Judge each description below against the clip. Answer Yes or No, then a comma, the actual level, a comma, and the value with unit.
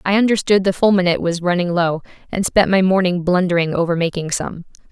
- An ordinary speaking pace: Yes, average, 185 wpm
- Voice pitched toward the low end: No, medium, 180 Hz